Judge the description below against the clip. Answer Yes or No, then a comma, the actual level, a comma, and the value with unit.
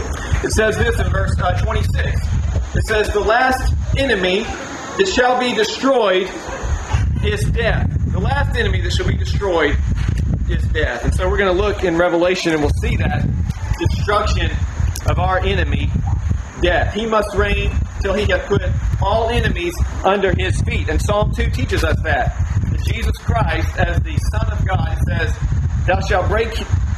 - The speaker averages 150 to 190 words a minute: Yes, average, 160 wpm